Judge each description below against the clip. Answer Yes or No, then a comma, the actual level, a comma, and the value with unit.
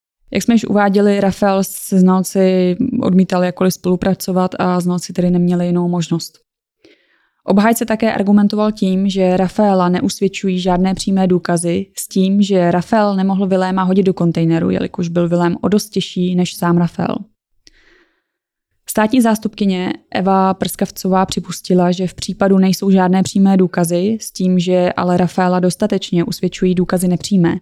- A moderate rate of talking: Yes, average, 140 wpm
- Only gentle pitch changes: Yes, narrow, 1.8 semitones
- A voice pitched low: No, medium, 185 Hz